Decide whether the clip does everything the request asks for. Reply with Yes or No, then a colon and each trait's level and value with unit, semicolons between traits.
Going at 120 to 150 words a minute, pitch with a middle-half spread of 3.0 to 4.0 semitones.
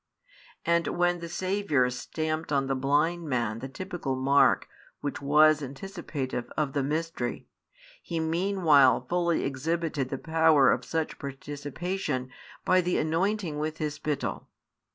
Yes: slow, 135 wpm; average, 3.7 semitones